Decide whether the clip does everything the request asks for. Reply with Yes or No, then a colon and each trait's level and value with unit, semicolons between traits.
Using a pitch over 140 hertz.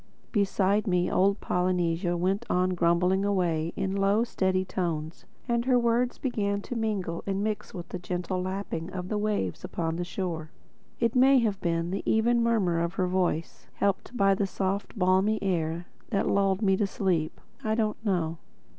Yes: high, 190 Hz